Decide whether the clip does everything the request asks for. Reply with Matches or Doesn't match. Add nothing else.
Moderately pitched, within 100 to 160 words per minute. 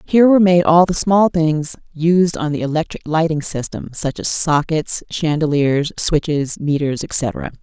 Matches